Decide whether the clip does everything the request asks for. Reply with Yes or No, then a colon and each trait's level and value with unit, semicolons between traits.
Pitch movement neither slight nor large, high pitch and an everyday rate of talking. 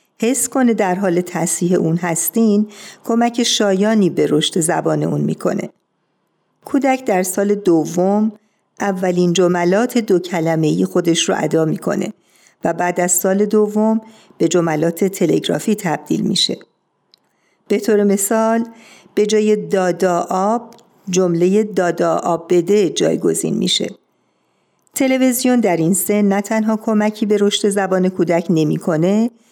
Yes: average, 3.6 semitones; high, 200 Hz; average, 125 wpm